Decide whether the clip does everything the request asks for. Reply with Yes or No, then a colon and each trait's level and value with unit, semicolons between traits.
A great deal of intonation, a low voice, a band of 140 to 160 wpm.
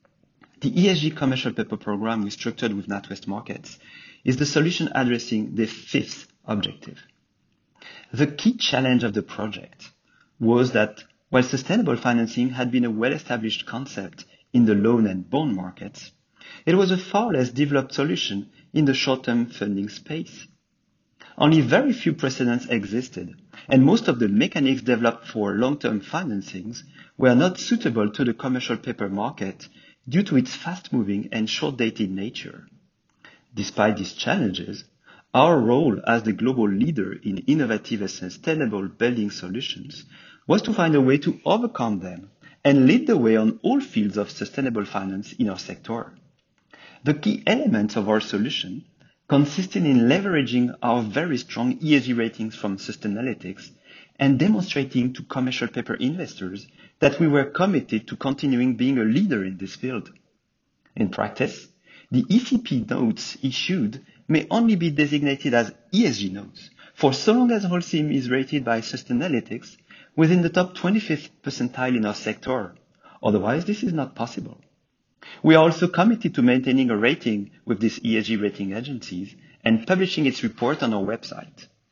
Yes: wide, 5.7 semitones; low, 125 Hz; average, 150 wpm